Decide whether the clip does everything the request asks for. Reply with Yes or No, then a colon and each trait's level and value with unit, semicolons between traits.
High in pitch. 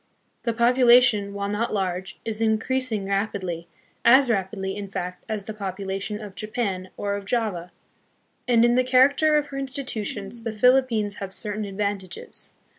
Yes: high, 210 Hz